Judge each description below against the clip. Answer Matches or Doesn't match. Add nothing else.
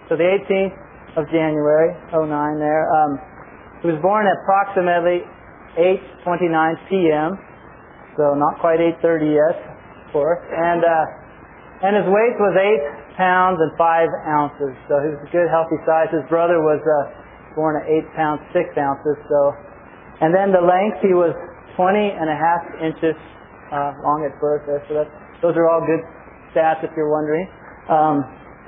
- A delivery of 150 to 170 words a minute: Matches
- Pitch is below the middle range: Doesn't match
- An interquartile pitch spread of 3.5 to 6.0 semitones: Doesn't match